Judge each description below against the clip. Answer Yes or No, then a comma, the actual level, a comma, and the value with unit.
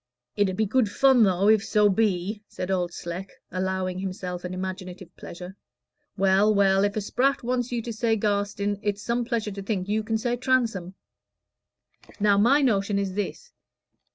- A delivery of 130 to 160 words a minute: No, average, 175 wpm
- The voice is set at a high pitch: Yes, high, 205 Hz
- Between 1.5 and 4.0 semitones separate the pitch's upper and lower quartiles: Yes, average, 2.9 semitones